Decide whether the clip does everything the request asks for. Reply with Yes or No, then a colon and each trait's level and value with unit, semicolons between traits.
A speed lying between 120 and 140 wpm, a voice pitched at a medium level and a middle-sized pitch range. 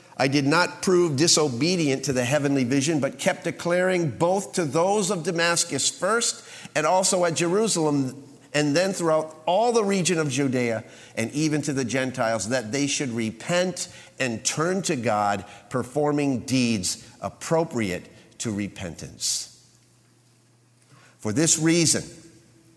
No: slow, 135 wpm; medium, 145 Hz; wide, 5.9 semitones